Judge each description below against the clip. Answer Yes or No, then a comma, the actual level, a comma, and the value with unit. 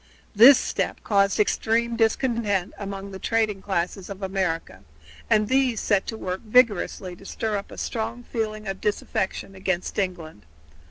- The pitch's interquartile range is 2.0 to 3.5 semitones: Yes, average, 2.8 semitones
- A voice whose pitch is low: No, high, 205 Hz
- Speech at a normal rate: Yes, average, 150 wpm